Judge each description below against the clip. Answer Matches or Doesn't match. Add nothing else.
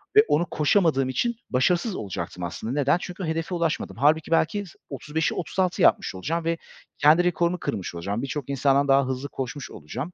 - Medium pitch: Matches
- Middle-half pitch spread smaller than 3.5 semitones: Doesn't match